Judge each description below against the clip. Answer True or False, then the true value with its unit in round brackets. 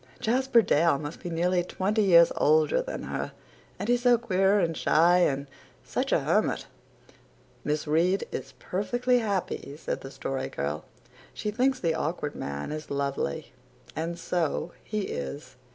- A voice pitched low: False (170 Hz)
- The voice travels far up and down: True (6.0 semitones)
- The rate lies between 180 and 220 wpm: False (150 wpm)